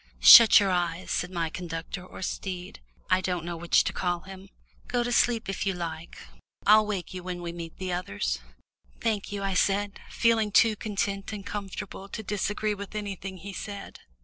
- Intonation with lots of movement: No, narrow, 2.6 semitones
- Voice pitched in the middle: No, high, 195 Hz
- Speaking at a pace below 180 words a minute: No, average, 185 wpm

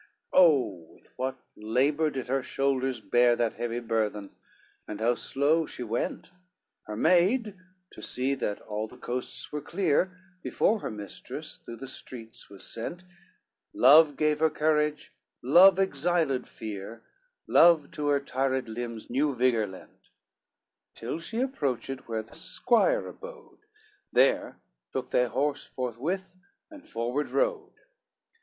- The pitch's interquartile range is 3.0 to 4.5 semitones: No, wide, 5.6 semitones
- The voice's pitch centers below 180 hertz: Yes, low, 135 Hz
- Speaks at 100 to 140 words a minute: Yes, slow, 135 wpm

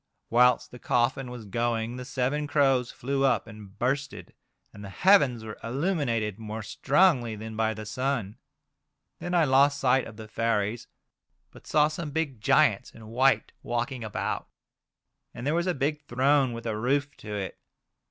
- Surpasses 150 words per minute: Yes, average, 165 wpm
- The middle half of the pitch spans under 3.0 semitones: No, average, 4.0 semitones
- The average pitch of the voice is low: Yes, low, 125 Hz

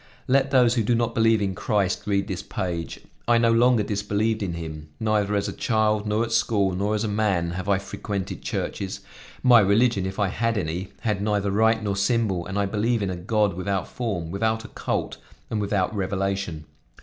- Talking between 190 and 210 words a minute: Yes, average, 200 wpm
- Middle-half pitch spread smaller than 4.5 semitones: Yes, average, 2.7 semitones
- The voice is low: Yes, low, 105 Hz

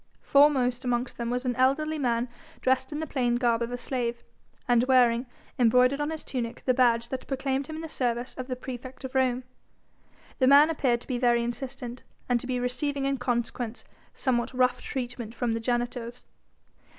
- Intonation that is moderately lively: No, narrow, 1.7 semitones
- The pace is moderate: Yes, average, 185 wpm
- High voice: Yes, very high, 250 Hz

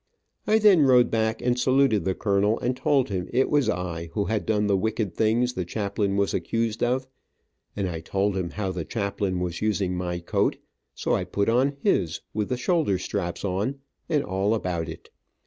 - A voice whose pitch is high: No, low, 105 Hz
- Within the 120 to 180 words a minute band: No, average, 195 wpm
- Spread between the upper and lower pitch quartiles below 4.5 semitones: No, average, 4.8 semitones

